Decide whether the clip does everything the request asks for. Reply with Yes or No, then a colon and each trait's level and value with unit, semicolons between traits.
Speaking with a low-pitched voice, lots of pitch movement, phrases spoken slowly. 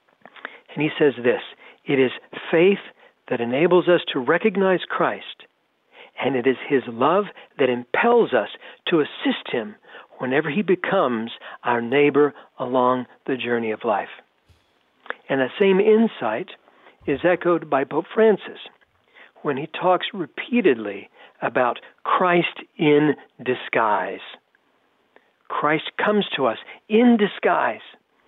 No: medium, 150 Hz; wide, 7.5 semitones; slow, 120 wpm